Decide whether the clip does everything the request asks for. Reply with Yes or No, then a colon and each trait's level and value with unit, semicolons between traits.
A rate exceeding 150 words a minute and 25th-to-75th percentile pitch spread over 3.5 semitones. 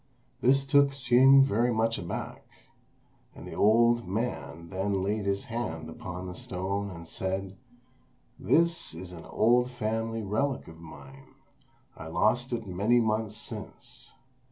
No: slow, 135 wpm; average, 4.7 semitones